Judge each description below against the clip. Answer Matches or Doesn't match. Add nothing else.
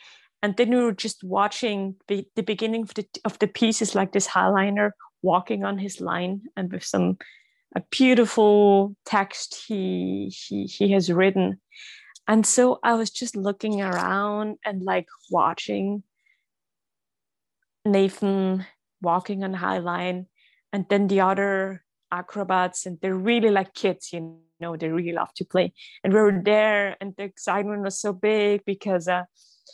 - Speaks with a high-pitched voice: Matches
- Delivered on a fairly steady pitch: Matches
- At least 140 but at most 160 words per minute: Matches